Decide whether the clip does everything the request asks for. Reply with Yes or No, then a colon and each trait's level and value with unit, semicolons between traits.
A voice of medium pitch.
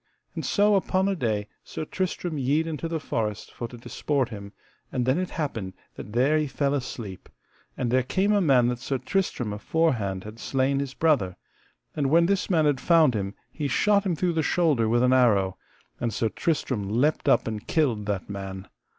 No: low, 130 Hz